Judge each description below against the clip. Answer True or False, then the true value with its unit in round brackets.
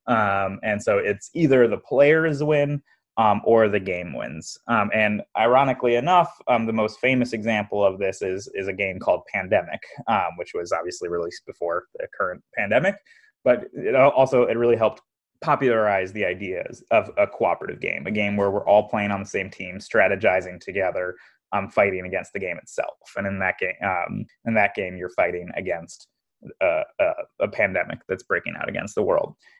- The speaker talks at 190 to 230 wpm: False (180 wpm)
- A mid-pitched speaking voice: False (115 Hz)